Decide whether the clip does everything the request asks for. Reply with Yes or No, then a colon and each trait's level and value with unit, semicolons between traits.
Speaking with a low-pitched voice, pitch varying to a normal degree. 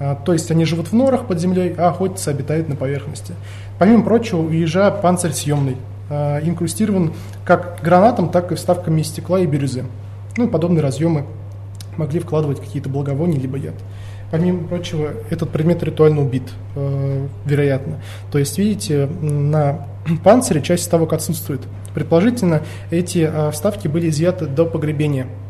No: medium, 155 Hz; average, 4.1 semitones